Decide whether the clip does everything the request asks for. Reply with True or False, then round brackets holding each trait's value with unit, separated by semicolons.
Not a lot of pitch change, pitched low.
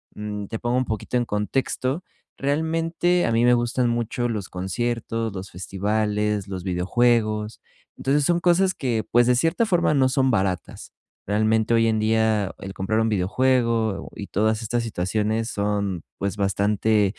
False (3.1 semitones; 110 Hz)